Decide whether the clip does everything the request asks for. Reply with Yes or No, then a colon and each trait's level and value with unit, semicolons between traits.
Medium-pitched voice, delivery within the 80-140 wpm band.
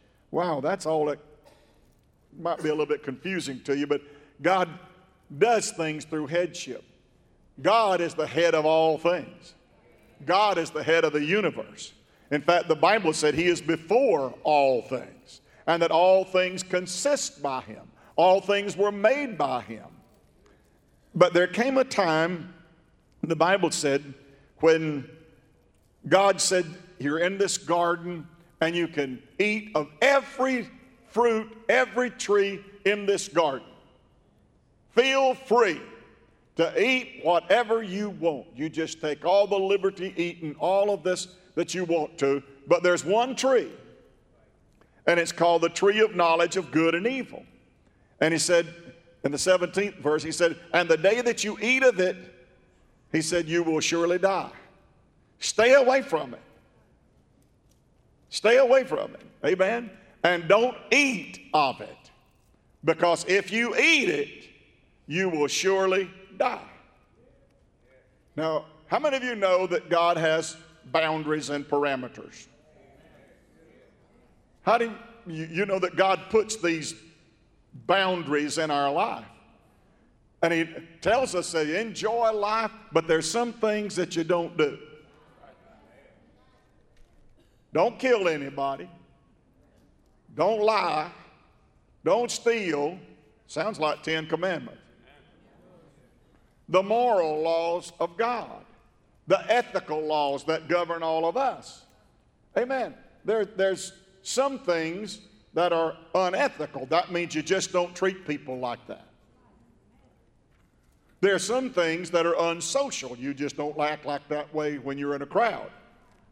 Yes: medium, 175 Hz; slow, 135 wpm